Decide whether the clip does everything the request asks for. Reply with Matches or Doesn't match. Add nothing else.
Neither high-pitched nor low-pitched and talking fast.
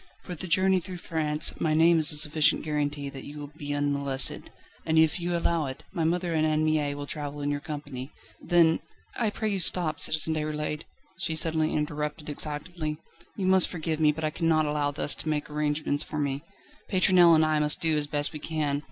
Matches